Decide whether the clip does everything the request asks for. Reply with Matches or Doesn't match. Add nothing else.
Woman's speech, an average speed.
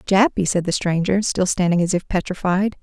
Matches